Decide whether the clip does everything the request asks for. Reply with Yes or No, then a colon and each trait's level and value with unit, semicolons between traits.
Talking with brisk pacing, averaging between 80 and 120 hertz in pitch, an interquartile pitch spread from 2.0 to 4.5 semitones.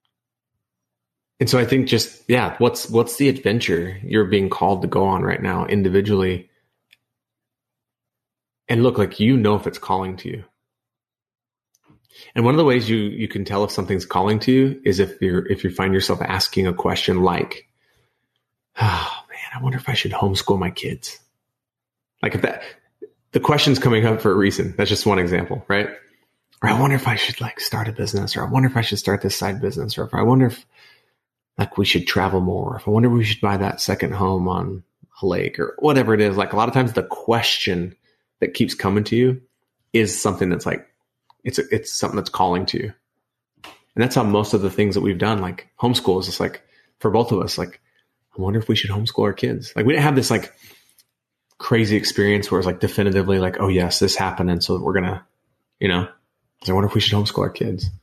Yes: fast, 215 wpm; low, 110 Hz; average, 4.2 semitones